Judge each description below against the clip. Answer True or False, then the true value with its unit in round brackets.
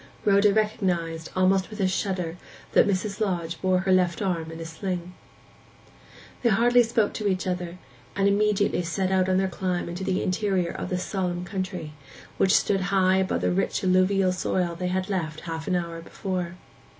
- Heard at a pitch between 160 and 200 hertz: True (185 Hz)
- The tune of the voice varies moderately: False (1.8 semitones)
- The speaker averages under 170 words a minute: False (180 wpm)